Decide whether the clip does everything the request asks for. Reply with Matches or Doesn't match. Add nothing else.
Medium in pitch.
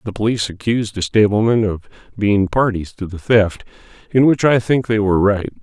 Doesn't match